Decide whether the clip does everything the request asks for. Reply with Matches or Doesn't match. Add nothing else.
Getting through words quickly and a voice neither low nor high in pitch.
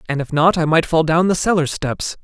Matches